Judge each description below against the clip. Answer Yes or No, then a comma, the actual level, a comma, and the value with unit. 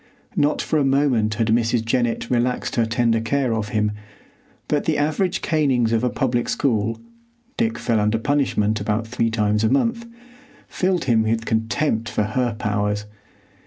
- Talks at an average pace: Yes, average, 155 wpm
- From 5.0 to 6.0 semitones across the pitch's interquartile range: No, average, 4.6 semitones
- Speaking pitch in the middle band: No, low, 120 Hz